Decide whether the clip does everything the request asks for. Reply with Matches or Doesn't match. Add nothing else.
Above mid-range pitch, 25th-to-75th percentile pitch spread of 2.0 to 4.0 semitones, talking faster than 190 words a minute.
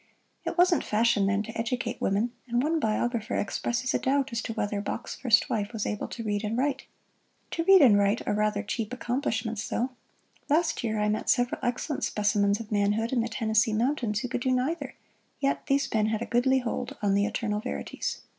Matches